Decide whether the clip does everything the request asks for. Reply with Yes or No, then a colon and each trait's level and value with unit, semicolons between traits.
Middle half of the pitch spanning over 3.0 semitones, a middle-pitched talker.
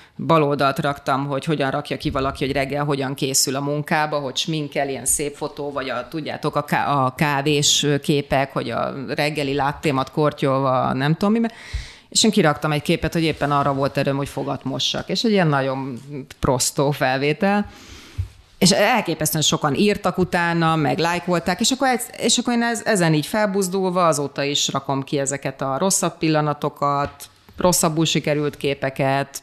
Yes: average, 3.5 semitones; medium, 150 Hz